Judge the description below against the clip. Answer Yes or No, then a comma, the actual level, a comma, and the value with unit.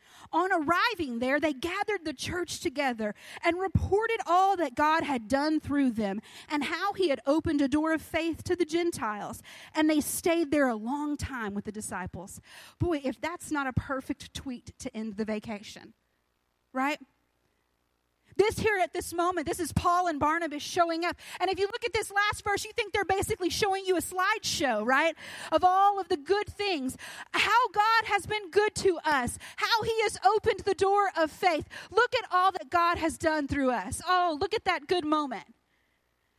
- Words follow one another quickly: No, average, 190 wpm